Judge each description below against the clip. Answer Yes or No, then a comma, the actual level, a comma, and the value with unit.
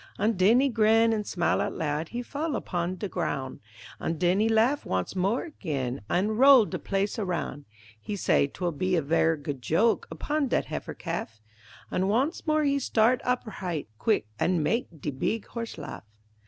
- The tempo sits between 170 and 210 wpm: Yes, average, 185 wpm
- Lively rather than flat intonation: Yes, wide, 6.1 semitones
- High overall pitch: Yes, high, 200 Hz